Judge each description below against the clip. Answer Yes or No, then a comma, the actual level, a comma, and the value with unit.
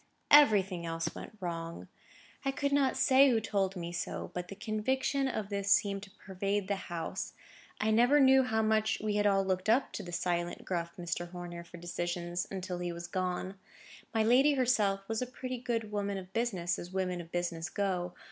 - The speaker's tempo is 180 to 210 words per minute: Yes, average, 190 wpm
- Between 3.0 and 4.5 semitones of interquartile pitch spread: Yes, average, 4.2 semitones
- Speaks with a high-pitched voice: Yes, high, 195 Hz